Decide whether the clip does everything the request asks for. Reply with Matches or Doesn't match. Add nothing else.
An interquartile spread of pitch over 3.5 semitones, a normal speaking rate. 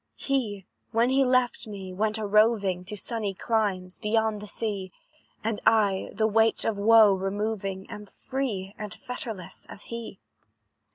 Doesn't match